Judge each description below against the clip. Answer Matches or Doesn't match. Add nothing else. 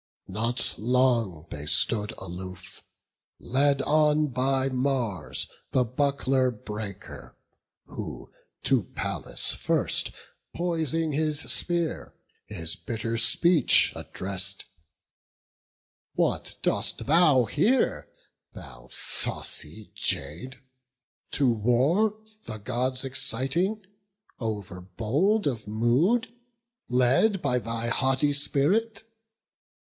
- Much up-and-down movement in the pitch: Matches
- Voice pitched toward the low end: Matches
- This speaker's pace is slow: Matches